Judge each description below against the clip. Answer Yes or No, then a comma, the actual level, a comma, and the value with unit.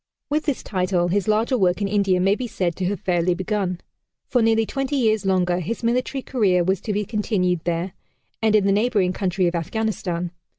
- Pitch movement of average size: Yes, average, 3.5 semitones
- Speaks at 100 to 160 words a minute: No, average, 200 wpm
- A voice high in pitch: Yes, high, 195 Hz